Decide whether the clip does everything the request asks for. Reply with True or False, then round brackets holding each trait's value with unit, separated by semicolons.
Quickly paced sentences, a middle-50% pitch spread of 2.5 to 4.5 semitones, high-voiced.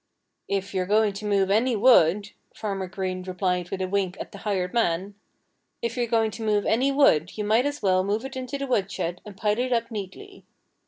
True (215 wpm; 3.6 semitones; 205 Hz)